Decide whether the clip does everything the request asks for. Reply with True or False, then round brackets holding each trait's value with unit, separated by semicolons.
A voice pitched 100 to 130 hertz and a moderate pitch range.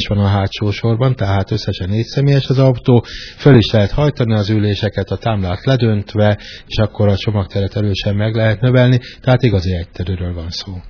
True (105 Hz; 3.4 semitones)